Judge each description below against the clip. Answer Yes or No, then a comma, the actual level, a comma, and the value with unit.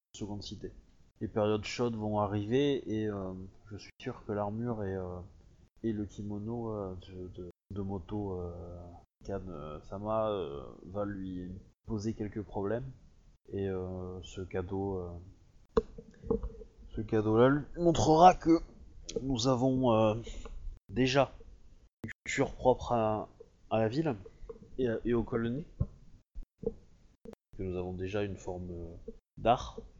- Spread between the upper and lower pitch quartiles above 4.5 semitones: No, average, 3.6 semitones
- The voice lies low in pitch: Yes, low, 105 Hz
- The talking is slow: Yes, slow, 130 wpm